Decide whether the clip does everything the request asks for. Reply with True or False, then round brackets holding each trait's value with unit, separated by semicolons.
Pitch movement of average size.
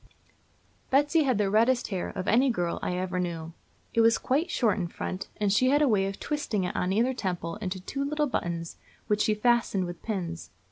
False (5.8 semitones)